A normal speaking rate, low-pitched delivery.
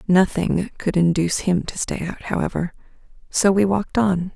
No: average, 165 wpm; medium, 185 Hz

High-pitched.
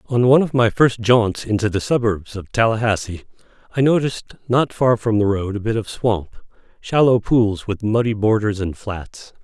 No: low, 110 Hz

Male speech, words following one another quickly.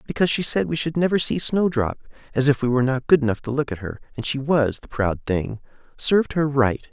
Yes: male; fast, 235 wpm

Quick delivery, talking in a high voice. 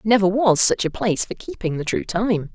Yes: fast, 235 wpm; high, 200 Hz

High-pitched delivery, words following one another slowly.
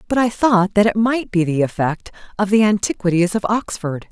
No: high, 200 Hz; fast, 205 wpm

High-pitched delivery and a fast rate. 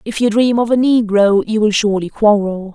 Yes: high, 215 Hz; fast, 220 wpm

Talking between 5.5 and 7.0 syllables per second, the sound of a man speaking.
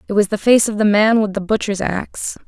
No: 5.8 syllables/s; female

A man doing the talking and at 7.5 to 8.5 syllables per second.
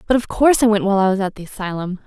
No: female; 8.0 syllables/s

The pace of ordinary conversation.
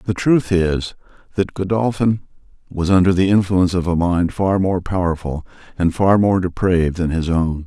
Yes: average, 170 wpm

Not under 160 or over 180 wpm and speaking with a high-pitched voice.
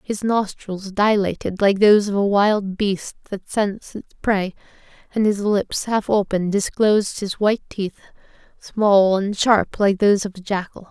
Yes: average, 165 wpm; high, 200 Hz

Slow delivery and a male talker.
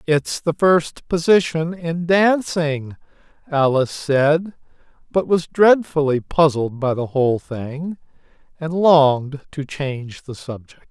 Yes: slow, 120 wpm; male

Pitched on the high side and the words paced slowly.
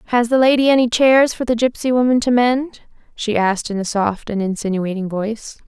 No: high, 230 Hz; average, 200 wpm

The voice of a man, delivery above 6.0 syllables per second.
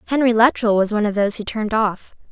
No: female; 7.1 syllables/s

